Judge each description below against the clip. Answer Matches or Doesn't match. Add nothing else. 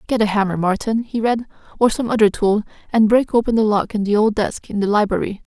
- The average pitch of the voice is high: Matches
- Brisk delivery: Matches